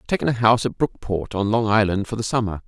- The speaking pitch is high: No, low, 110 Hz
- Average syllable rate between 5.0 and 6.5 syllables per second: No, 6.9 syllables/s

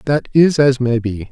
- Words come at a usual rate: No, fast, 230 wpm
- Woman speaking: No, male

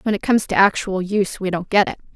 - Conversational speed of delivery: No, fast, 280 wpm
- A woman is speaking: Yes, female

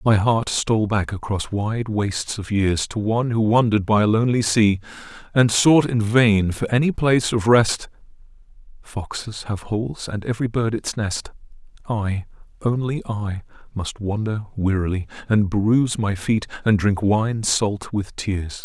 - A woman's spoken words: No, male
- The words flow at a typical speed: Yes, average, 160 wpm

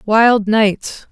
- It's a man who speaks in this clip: No, female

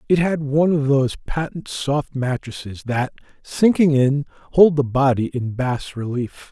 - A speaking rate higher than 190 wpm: No, average, 155 wpm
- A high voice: No, medium, 140 Hz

